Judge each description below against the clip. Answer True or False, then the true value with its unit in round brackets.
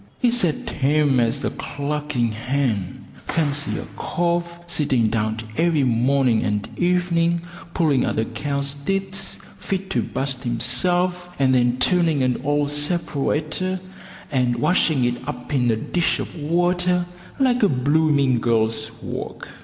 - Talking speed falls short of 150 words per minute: True (135 wpm)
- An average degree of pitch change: False (5.7 semitones)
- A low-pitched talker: False (145 Hz)